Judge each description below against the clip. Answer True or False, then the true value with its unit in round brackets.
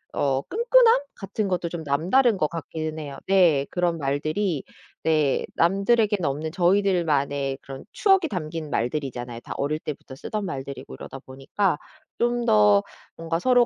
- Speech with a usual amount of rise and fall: False (5.9 semitones)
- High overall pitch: False (160 Hz)